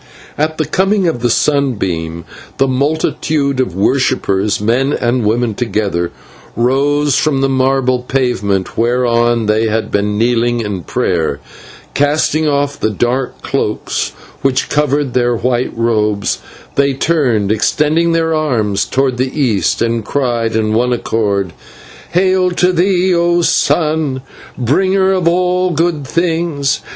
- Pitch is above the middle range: No, low, 130 Hz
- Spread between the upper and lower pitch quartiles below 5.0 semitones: No, average, 5.3 semitones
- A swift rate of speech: No, slow, 135 wpm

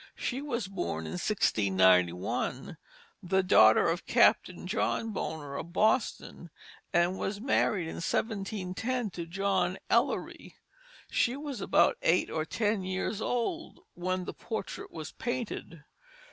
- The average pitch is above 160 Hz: Yes, high, 190 Hz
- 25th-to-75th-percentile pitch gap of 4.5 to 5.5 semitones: Yes, average, 5.1 semitones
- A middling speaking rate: No, slow, 125 wpm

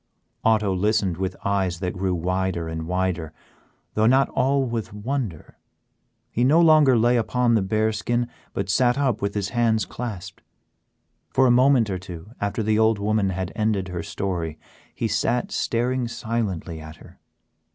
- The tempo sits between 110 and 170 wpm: Yes, average, 160 wpm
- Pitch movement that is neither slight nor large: Yes, average, 4.3 semitones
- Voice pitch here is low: Yes, low, 105 Hz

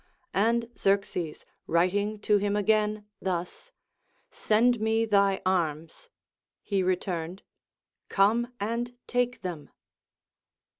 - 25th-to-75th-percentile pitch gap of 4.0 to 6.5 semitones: No, average, 3.3 semitones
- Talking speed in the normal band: No, slow, 95 wpm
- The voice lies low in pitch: No, high, 205 Hz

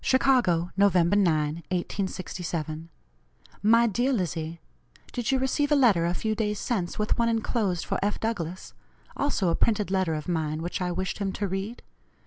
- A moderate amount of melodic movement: Yes, average, 4.9 semitones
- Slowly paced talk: No, average, 165 wpm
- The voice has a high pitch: Yes, high, 195 Hz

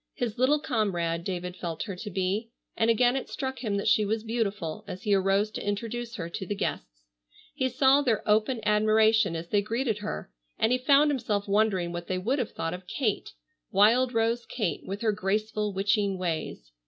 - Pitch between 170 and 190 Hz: No, high, 210 Hz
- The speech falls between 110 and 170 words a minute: No, average, 195 wpm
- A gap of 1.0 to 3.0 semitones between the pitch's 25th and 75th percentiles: No, average, 3.5 semitones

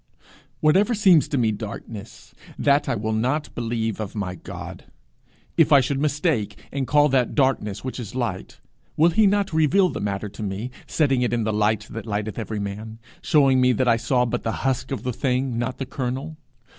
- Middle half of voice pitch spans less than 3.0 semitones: No, average, 4.6 semitones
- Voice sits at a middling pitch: No, low, 125 Hz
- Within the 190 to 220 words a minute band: Yes, average, 195 wpm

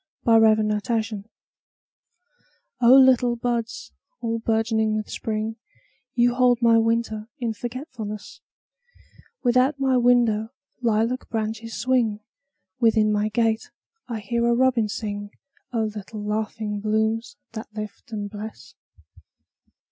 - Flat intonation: Yes, narrow, 2.1 semitones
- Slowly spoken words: Yes, slow, 105 wpm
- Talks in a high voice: Yes, high, 225 Hz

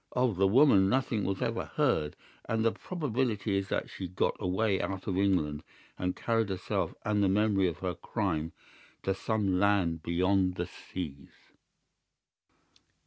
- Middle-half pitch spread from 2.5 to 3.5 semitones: Yes, average, 2.9 semitones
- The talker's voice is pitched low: Yes, very low, 95 Hz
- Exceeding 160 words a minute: No, average, 150 wpm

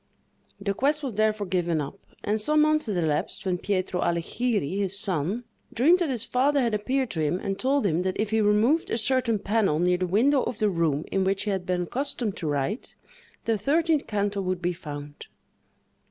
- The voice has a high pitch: Yes, high, 205 Hz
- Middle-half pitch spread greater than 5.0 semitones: Yes, wide, 5.5 semitones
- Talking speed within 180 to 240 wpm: Yes, average, 200 wpm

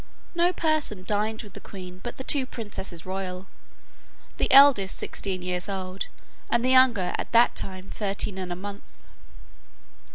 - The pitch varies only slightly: No, average, 4.6 semitones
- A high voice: Yes, high, 200 Hz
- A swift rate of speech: No, average, 155 wpm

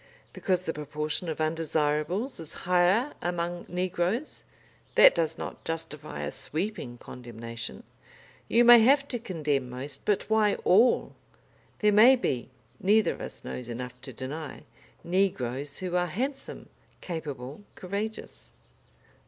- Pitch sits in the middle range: Yes, medium, 175 Hz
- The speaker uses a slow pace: Yes, slow, 130 wpm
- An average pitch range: No, wide, 6.4 semitones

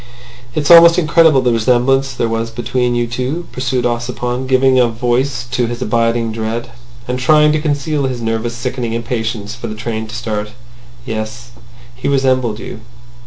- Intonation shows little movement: Yes, narrow, 2.3 semitones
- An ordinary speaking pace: Yes, average, 165 wpm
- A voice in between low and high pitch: No, low, 120 Hz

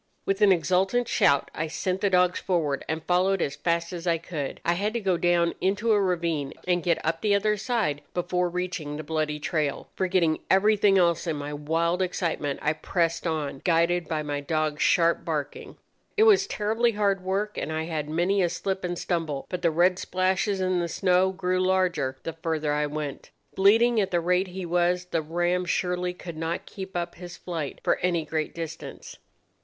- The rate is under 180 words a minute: No, average, 195 wpm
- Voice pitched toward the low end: No, medium, 175 Hz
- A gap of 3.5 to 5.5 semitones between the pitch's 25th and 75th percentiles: No, average, 2.9 semitones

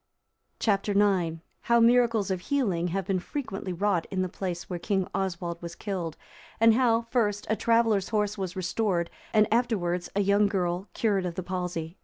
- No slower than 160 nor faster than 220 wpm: Yes, average, 175 wpm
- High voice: Yes, high, 195 Hz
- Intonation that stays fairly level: No, average, 3.5 semitones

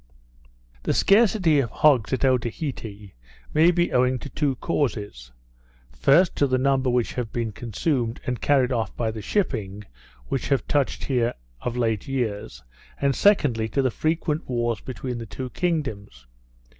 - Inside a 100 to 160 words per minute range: Yes, average, 155 wpm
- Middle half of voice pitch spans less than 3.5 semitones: No, average, 4.3 semitones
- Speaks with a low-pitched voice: Yes, low, 125 Hz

